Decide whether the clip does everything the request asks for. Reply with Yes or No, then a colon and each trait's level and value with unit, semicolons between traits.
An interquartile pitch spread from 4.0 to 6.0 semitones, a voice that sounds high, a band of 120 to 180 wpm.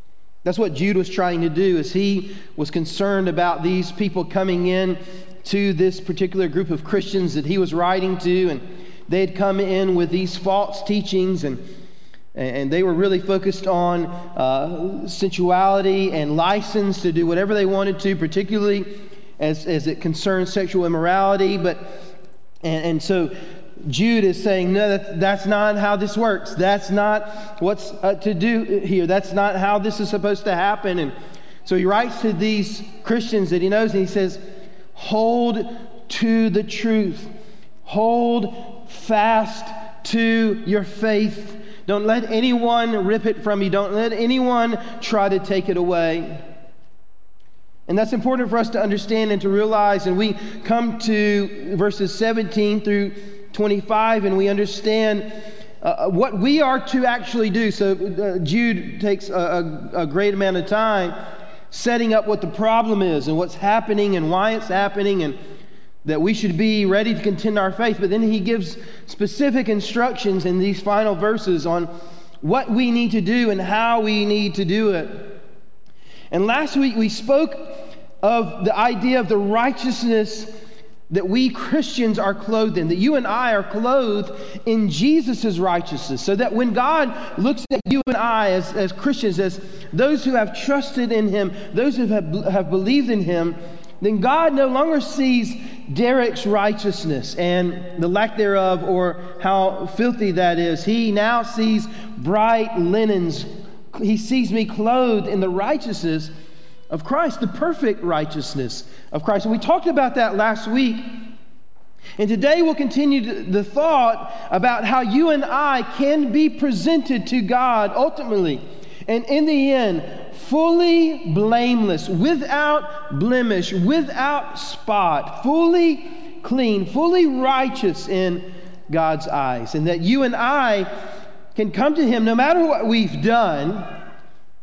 No: average, 3.6 semitones; high, 205 Hz; average, 155 wpm